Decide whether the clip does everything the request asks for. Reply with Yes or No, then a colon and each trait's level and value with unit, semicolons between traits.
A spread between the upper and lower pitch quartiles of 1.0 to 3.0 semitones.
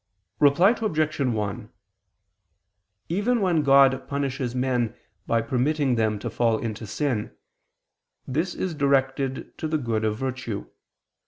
No: average, 4.5 semitones